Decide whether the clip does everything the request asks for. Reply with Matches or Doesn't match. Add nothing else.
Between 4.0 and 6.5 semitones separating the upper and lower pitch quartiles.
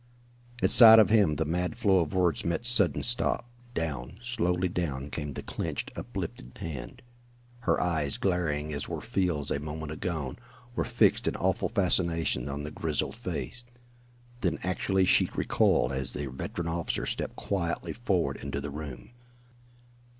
Matches